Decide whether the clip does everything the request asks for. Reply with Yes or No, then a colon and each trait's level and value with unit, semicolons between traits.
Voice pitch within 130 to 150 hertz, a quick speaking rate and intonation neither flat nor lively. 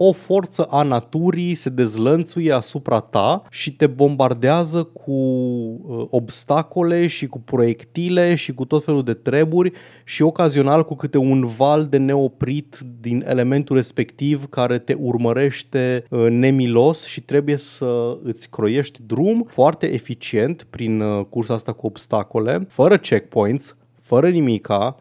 No: low, 135 Hz; average, 130 wpm; average, 4.2 semitones